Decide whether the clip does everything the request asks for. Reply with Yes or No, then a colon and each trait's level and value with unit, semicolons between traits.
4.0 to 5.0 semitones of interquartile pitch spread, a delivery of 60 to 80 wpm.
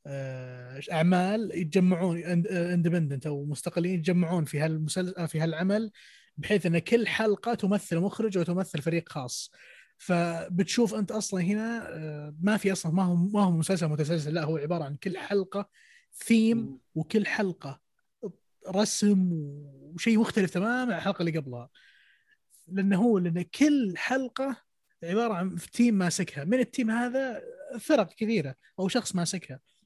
No: average, 4.7 semitones; fast, 135 wpm